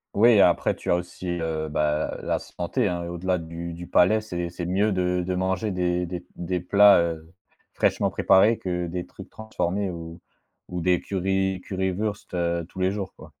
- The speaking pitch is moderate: No, very low, 90 Hz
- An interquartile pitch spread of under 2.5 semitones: Yes, narrow, 1.9 semitones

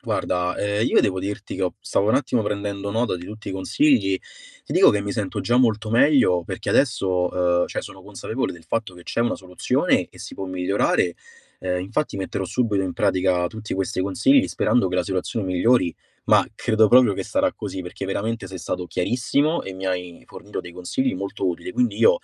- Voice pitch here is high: No, low, 100 Hz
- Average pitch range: Yes, average, 3.7 semitones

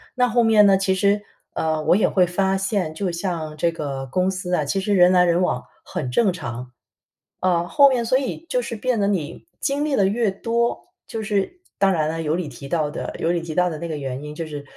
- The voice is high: No, medium, 180 Hz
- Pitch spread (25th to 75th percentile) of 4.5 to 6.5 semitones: Yes, average, 4.8 semitones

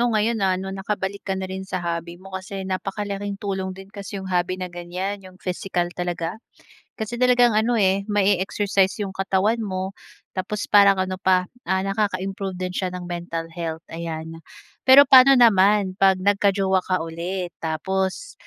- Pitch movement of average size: No, narrow, 1.7 semitones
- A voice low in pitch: No, high, 190 Hz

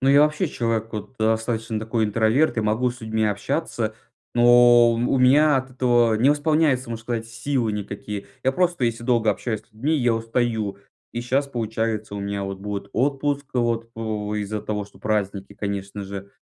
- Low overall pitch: Yes, low, 115 Hz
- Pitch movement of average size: Yes, average, 3.1 semitones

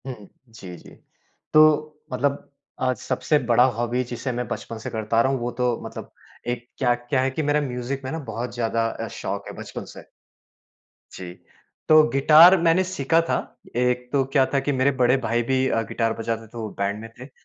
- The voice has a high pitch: No, low, 125 Hz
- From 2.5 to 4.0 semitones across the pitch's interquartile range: Yes, average, 3.0 semitones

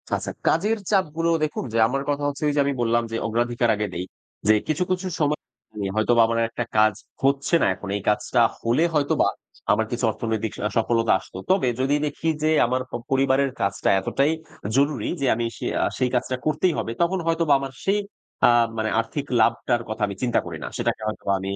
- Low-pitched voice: Yes, low, 130 Hz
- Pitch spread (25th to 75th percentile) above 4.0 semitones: Yes, average, 4.8 semitones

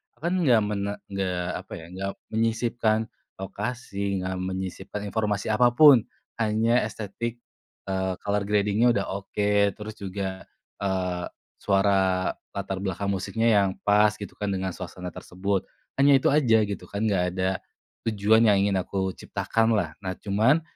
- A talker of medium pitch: No, low, 100 Hz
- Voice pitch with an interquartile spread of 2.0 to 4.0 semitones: Yes, average, 2.7 semitones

